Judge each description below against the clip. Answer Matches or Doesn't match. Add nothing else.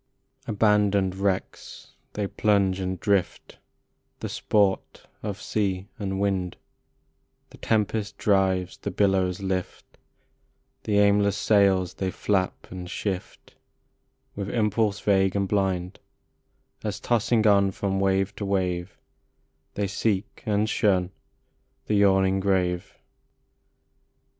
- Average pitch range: Doesn't match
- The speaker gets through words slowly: Matches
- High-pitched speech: Doesn't match